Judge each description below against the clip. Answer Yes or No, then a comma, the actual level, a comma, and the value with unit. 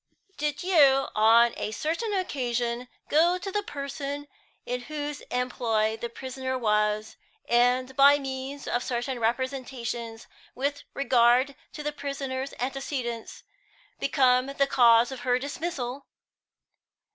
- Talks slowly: Yes, slow, 120 wpm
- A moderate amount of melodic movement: Yes, average, 3.0 semitones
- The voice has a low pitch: No, very high, 260 Hz